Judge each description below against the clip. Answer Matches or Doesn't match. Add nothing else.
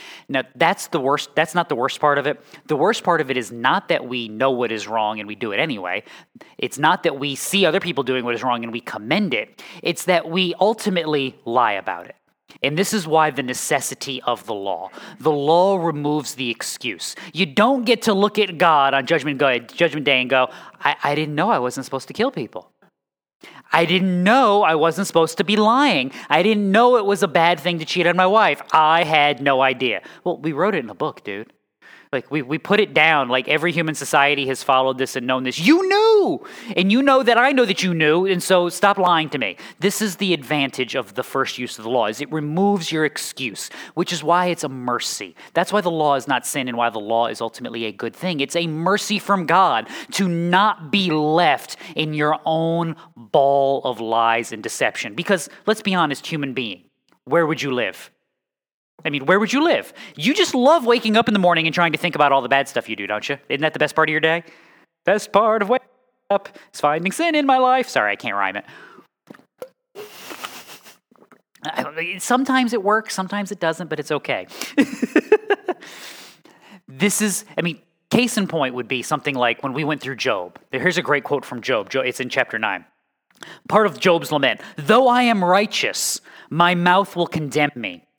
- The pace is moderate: Doesn't match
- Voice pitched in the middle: Matches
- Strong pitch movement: Matches